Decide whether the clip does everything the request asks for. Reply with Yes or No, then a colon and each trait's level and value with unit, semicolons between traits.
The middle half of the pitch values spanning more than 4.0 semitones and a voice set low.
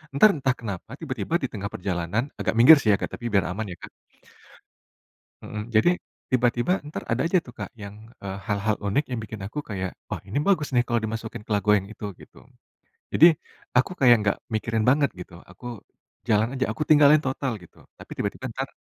Yes: average, 4.5 semitones; low, 115 Hz